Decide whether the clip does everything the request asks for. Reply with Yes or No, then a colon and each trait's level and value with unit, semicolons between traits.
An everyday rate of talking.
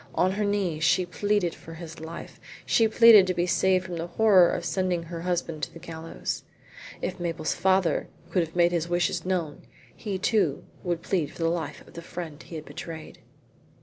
Yes: average, 190 wpm